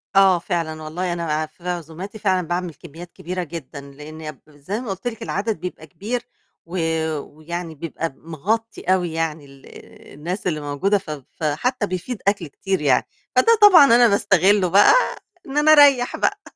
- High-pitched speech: No, medium, 175 Hz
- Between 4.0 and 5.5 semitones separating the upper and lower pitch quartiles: Yes, average, 4.5 semitones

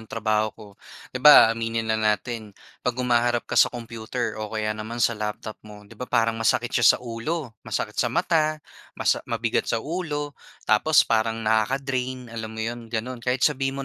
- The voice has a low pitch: Yes, low, 115 Hz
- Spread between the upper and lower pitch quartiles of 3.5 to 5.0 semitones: No, narrow, 2.6 semitones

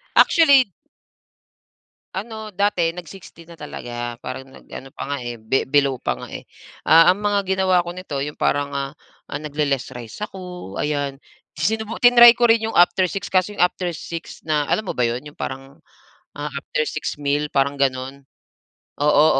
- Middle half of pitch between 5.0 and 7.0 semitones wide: Yes, wide, 5.5 semitones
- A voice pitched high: No, medium, 155 Hz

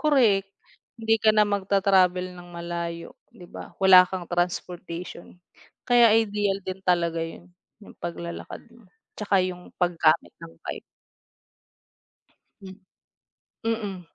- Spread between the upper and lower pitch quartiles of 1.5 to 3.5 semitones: Yes, average, 2.9 semitones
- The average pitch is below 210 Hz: Yes, medium, 185 Hz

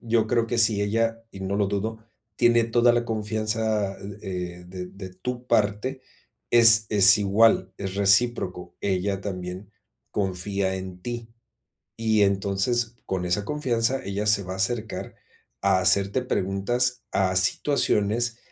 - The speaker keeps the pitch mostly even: No, average, 3.2 semitones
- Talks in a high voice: No, low, 105 Hz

